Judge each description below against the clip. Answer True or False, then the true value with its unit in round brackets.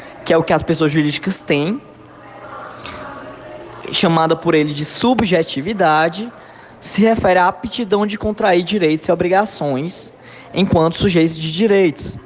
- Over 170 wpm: False (125 wpm)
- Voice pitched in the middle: True (170 Hz)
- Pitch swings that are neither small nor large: True (4.4 semitones)